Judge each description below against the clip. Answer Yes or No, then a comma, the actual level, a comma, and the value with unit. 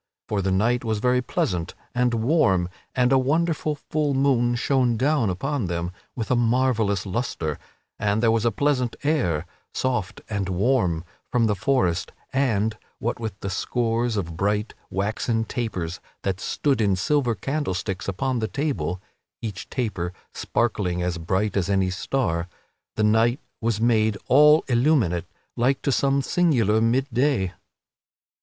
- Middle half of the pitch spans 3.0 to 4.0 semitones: No, average, 5.2 semitones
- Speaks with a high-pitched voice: No, low, 115 Hz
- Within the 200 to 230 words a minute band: No, average, 150 wpm